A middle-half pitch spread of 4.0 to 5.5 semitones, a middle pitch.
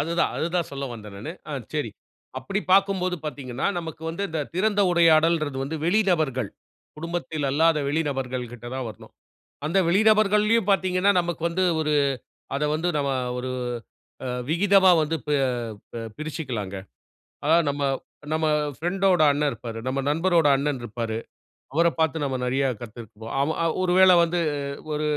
Yes: average, 4.6 semitones; medium, 160 Hz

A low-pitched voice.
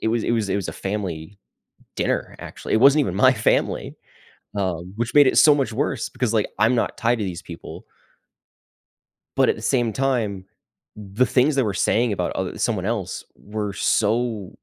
Yes: low, 110 Hz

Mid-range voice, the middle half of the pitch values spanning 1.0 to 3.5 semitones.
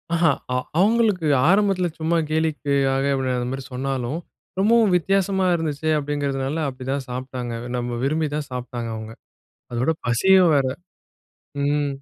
No: medium, 145 Hz; average, 4.8 semitones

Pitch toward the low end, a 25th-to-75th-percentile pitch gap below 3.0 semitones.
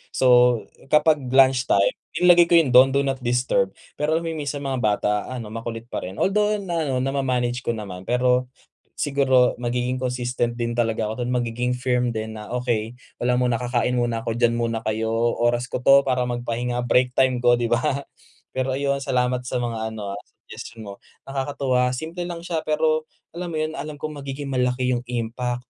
Yes: low, 125 Hz; narrow, 2.4 semitones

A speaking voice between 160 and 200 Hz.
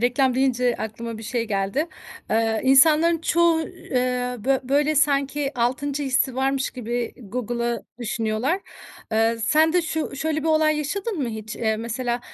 No: very high, 255 Hz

